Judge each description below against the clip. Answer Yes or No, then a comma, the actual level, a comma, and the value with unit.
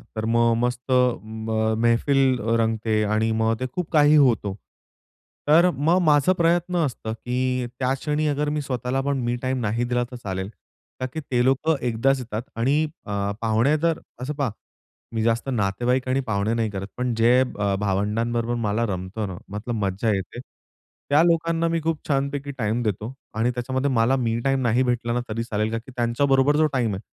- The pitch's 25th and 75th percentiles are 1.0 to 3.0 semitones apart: No, average, 3.6 semitones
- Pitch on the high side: No, low, 120 Hz